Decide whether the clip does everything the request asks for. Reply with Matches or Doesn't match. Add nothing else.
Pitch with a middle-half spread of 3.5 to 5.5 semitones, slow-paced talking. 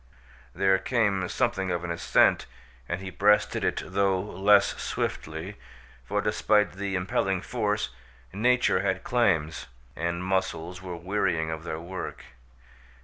Doesn't match